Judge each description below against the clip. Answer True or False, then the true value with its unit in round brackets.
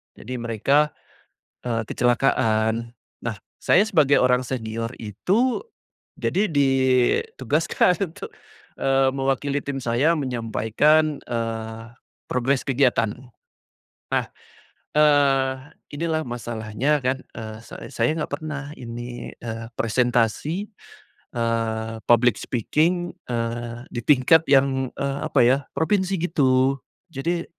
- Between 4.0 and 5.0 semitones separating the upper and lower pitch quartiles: True (4.3 semitones)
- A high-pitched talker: False (130 Hz)